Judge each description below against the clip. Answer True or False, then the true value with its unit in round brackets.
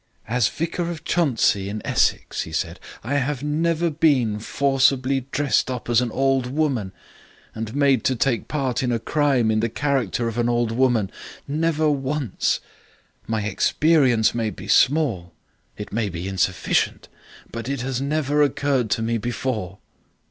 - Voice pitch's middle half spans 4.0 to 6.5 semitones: True (4.3 semitones)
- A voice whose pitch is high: False (130 Hz)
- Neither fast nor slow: True (155 wpm)